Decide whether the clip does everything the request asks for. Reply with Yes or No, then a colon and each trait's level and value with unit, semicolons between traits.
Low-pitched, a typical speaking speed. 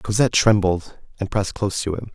Yes: low, 100 Hz; average, 195 wpm